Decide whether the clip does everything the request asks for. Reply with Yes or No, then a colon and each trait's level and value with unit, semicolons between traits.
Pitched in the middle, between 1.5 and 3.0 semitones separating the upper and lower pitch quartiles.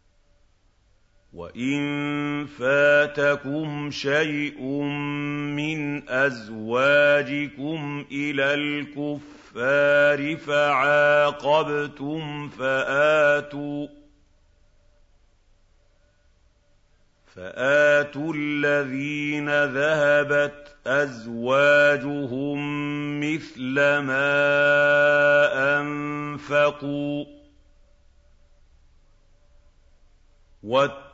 No: medium, 145 Hz; average, 5.1 semitones